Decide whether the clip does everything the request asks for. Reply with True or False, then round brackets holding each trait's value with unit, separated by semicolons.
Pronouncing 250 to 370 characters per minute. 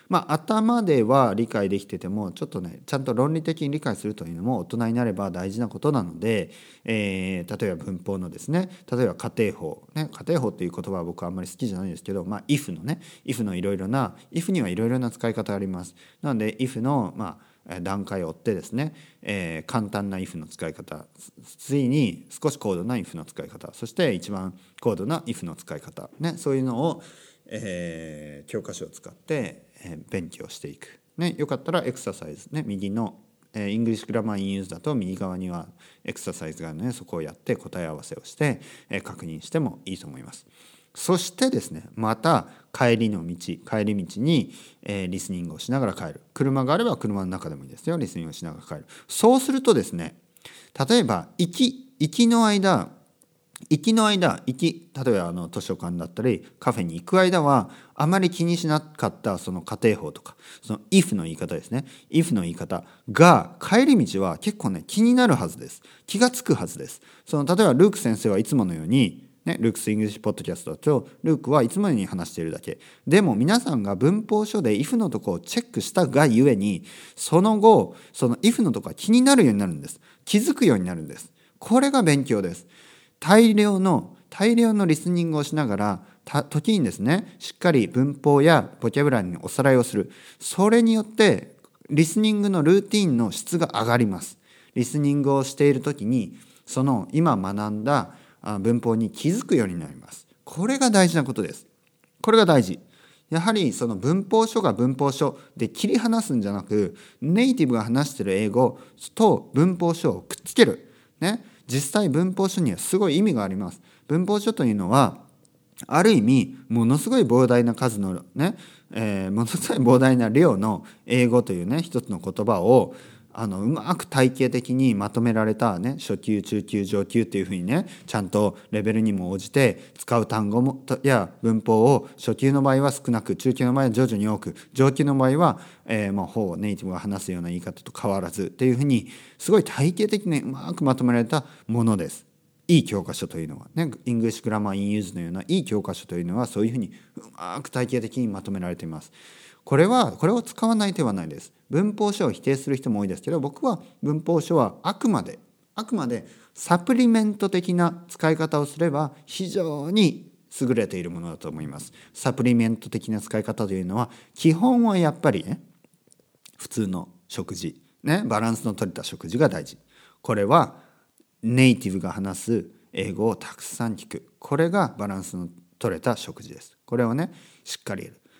False (385 characters per minute)